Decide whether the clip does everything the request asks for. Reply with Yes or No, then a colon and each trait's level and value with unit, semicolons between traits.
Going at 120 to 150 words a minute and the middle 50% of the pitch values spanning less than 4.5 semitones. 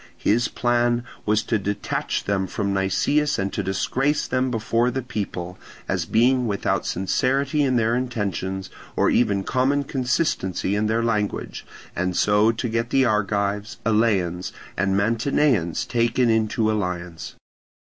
Yes: slow, 135 wpm; average, 3.9 semitones